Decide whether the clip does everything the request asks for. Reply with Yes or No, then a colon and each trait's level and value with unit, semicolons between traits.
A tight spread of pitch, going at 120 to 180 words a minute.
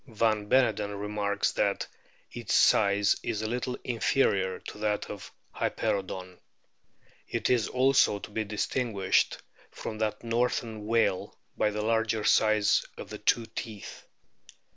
Yes: narrow, 2.0 semitones; slow, 135 wpm